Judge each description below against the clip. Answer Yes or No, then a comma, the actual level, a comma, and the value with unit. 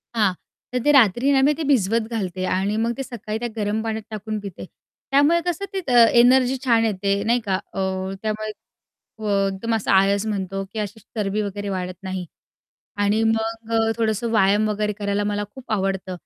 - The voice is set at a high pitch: Yes, high, 215 Hz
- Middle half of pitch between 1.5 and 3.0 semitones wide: Yes, average, 2.7 semitones